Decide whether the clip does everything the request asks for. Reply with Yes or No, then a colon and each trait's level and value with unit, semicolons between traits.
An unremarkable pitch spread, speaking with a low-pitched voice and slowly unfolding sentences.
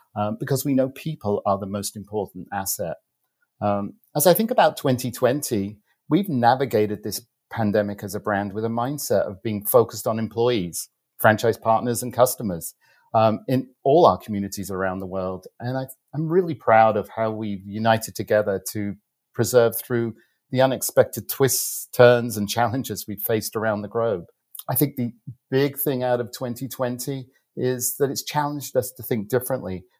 No: average, 4.2 semitones; low, 115 Hz; average, 165 wpm